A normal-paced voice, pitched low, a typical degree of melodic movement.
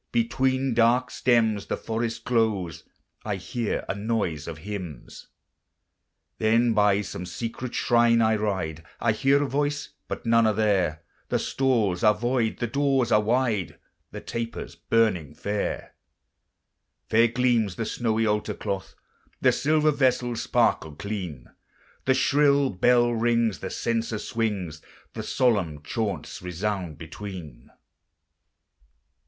No: slow, 125 wpm; low, 110 Hz; average, 3.8 semitones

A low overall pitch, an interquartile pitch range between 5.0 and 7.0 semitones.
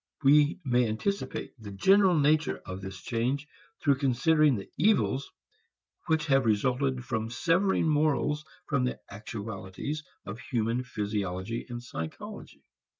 Yes: low, 125 Hz; wide, 5.5 semitones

